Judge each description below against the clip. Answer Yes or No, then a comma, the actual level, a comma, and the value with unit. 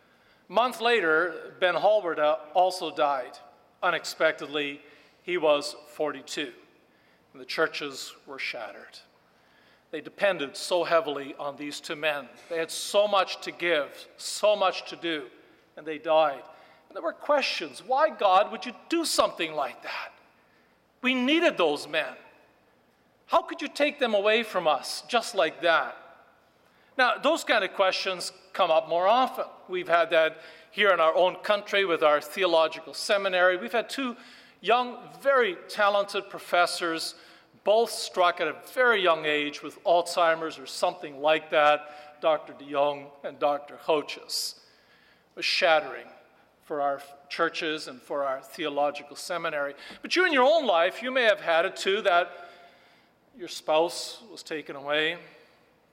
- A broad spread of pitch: Yes, wide, 6.3 semitones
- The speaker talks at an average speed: Yes, average, 150 wpm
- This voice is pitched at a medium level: Yes, medium, 175 Hz